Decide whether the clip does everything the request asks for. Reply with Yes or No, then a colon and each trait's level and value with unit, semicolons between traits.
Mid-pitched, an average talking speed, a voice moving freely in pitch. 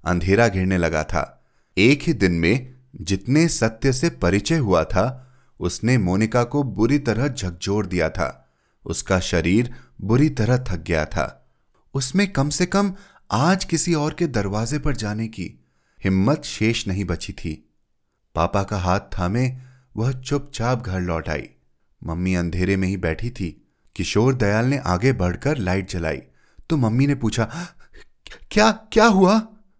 No: low, 110 Hz; average, 150 wpm; wide, 7.2 semitones